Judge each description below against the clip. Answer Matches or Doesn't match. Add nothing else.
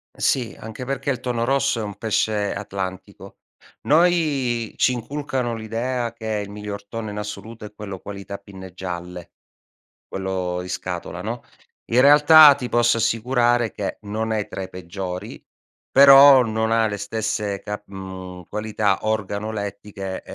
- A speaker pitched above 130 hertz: Doesn't match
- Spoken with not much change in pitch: Doesn't match